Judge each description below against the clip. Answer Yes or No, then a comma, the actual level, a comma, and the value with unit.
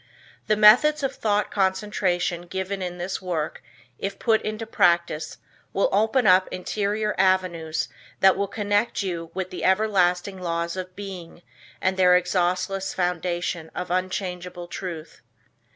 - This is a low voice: No, medium, 185 Hz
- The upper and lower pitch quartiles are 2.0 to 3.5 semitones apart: Yes, narrow, 2.4 semitones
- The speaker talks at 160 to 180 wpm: No, slow, 135 wpm